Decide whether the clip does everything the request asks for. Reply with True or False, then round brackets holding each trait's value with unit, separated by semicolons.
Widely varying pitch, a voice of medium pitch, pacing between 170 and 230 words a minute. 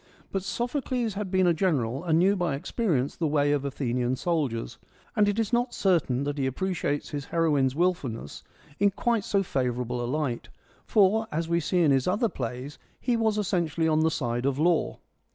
True (6.4 semitones; 160 Hz; 190 wpm)